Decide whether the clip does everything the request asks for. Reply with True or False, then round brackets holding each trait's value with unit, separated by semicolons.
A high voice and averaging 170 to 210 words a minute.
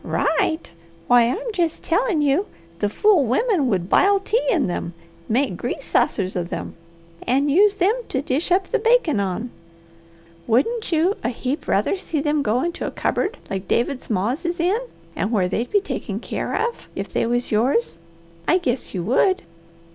True (290 Hz; 175 wpm)